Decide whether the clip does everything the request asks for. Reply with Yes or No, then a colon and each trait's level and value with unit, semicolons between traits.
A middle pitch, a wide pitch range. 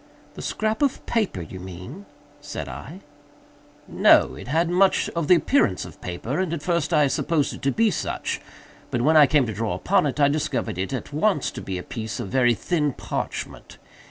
Yes: medium, 145 Hz; wide, 7.7 semitones